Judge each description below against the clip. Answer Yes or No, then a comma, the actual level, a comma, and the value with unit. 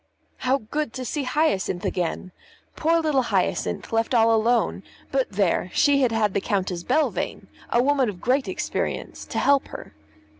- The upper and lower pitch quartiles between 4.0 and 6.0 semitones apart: Yes, average, 4.6 semitones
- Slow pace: No, average, 160 wpm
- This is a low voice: No, very high, 250 Hz